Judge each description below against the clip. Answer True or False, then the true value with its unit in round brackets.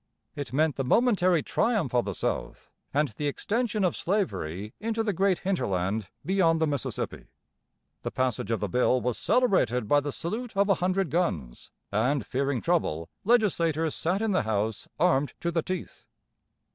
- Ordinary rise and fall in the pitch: False (7.6 semitones)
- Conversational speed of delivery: True (165 wpm)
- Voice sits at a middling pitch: True (160 Hz)